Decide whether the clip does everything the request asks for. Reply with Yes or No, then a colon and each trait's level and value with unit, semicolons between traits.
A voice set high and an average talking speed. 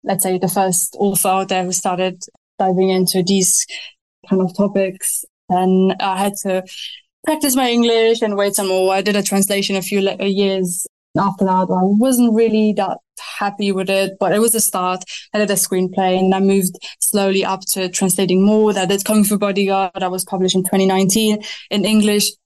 Yes: high, 195 Hz; average, 190 wpm